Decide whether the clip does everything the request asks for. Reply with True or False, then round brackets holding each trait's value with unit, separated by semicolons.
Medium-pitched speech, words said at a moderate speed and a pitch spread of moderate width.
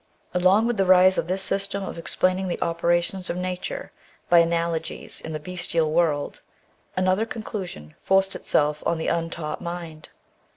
False (175 Hz; 155 wpm; 2.2 semitones)